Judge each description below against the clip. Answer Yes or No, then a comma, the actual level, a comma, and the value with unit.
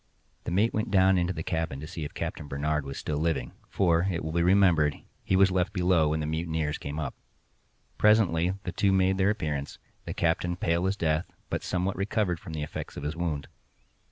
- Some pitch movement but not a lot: Yes, average, 3.4 semitones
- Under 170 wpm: No, fast, 205 wpm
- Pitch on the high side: No, very low, 85 Hz